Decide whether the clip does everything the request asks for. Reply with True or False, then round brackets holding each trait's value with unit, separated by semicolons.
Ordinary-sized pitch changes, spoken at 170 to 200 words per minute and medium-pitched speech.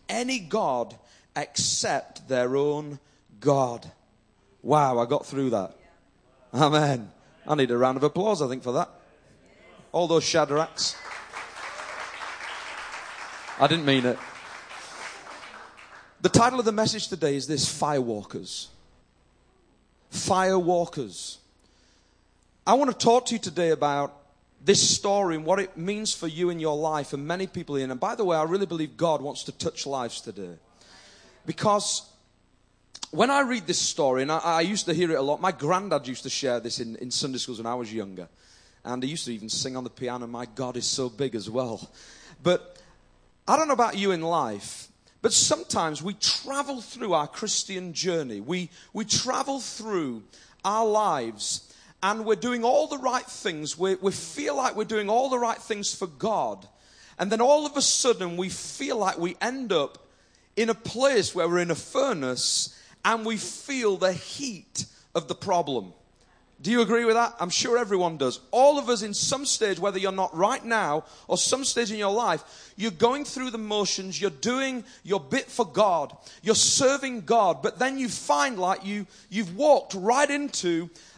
False (8.0 semitones; 175 wpm; 180 Hz)